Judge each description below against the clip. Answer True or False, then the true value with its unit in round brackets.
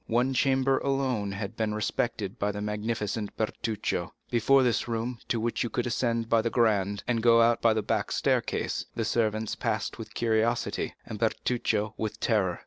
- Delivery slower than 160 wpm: False (175 wpm)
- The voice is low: True (115 Hz)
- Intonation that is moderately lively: False (2.0 semitones)